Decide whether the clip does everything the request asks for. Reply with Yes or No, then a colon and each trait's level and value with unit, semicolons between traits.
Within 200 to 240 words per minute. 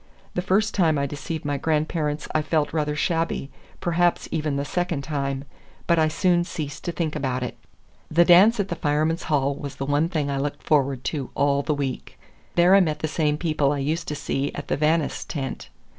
Yes: fast, 205 wpm